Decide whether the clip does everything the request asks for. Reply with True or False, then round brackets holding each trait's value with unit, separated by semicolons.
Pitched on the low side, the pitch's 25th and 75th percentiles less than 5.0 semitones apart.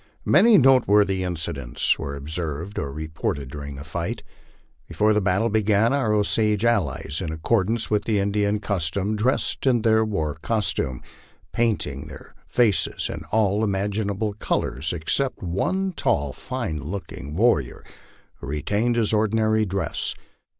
False (100 Hz; 5.6 semitones)